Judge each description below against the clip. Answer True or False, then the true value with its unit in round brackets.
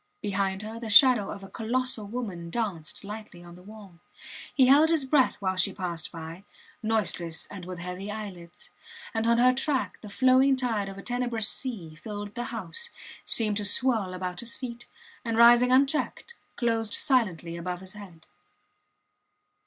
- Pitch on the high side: True (210 Hz)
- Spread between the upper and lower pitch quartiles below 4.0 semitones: False (4.7 semitones)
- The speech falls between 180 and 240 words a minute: False (165 wpm)